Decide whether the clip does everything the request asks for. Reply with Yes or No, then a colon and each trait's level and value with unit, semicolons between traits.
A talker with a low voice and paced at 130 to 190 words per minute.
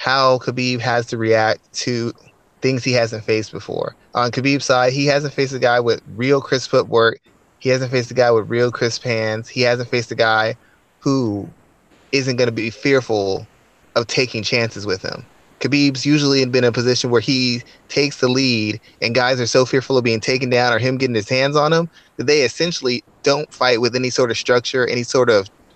No: low, 125 Hz; fast, 205 wpm